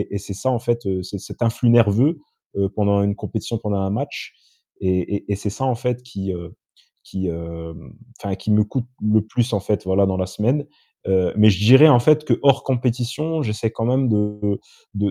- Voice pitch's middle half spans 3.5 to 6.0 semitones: Yes, average, 3.9 semitones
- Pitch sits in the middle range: No, low, 105 Hz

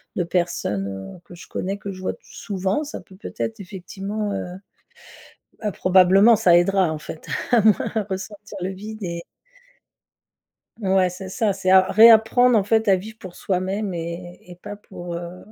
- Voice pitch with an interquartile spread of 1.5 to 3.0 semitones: Yes, average, 2.7 semitones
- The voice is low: No, high, 190 Hz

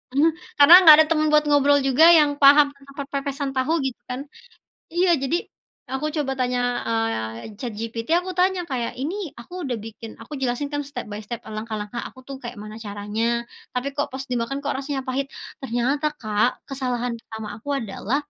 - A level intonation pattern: No, average, 3.9 semitones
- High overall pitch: Yes, very high, 265 Hz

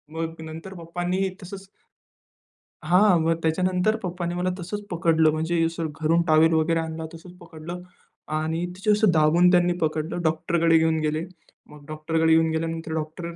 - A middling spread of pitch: No, narrow, 1.8 semitones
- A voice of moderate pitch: Yes, medium, 165 Hz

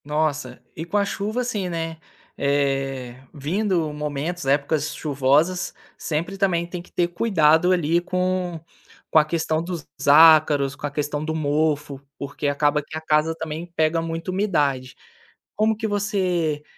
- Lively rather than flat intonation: No, average, 3.3 semitones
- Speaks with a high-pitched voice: No, medium, 160 Hz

